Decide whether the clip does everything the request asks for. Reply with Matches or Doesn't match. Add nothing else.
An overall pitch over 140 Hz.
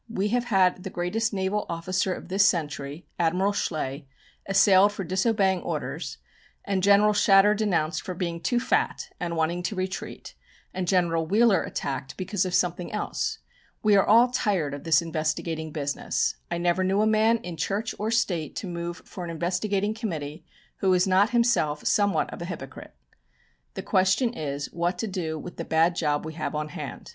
Matches